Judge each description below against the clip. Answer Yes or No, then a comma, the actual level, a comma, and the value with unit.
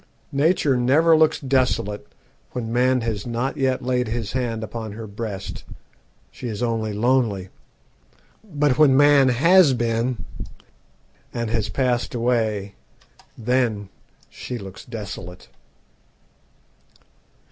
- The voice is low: Yes, low, 120 Hz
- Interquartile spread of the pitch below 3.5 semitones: Yes, average, 3.1 semitones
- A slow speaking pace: Yes, slow, 110 wpm